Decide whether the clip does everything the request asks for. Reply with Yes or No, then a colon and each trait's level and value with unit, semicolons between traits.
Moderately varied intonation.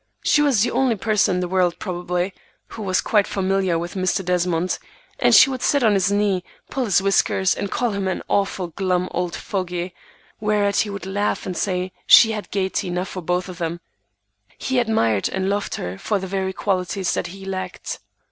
No: narrow, 2.2 semitones